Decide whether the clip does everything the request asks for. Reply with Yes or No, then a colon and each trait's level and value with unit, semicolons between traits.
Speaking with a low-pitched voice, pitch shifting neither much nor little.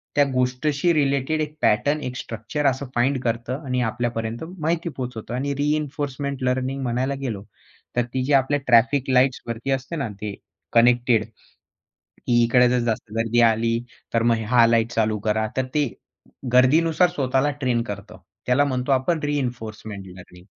Yes: low, 125 Hz; average, 3.3 semitones